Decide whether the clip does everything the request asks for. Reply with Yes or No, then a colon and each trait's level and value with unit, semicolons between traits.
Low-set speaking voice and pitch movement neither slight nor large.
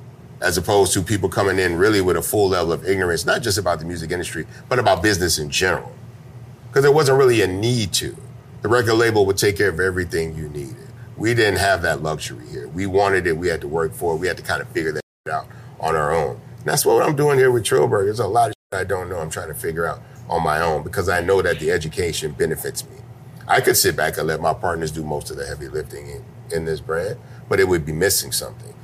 No: low, 120 Hz; wide, 6.0 semitones